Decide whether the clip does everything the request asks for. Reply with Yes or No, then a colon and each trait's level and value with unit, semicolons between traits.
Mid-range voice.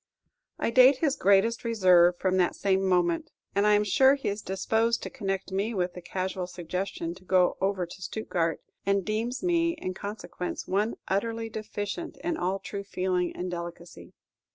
No: high, 195 Hz